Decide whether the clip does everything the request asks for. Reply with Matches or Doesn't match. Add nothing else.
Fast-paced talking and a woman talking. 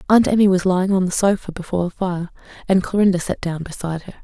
Matches